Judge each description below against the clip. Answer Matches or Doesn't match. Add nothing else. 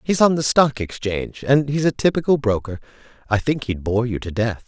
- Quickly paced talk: Matches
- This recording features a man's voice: Matches